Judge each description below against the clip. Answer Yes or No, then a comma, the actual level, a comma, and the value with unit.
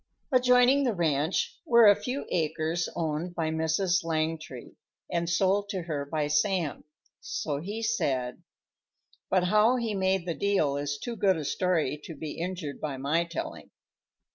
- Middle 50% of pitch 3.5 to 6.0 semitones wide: Yes, average, 4.6 semitones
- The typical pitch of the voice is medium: Yes, medium, 170 Hz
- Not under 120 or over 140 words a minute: No, average, 155 wpm